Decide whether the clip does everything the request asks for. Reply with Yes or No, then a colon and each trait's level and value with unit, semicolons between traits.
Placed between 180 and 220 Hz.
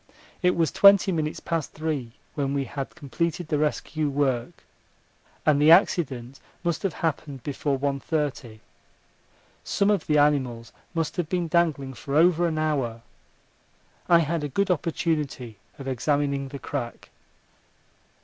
No: medium, 150 Hz